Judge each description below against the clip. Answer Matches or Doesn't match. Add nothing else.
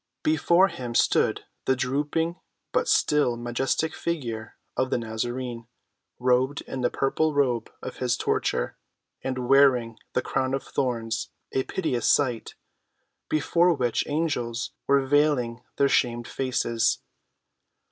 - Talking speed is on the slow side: Matches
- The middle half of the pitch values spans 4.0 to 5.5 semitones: Doesn't match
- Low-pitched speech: Matches